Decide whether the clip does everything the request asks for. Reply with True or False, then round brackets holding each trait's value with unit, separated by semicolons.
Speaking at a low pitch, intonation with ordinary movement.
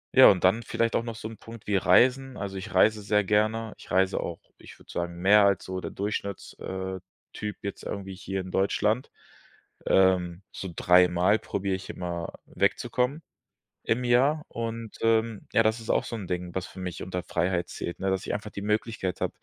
True (100 Hz; 3.2 semitones)